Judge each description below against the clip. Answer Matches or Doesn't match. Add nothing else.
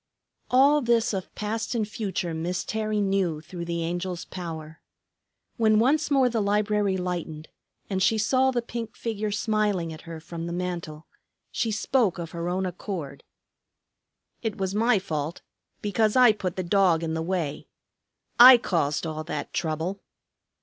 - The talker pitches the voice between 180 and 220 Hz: Matches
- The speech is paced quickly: Doesn't match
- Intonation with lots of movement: Doesn't match